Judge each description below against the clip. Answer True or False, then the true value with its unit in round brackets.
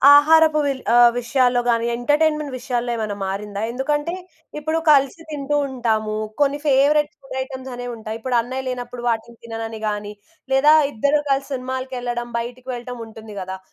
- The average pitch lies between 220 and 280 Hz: True (250 Hz)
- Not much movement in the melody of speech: False (3.2 semitones)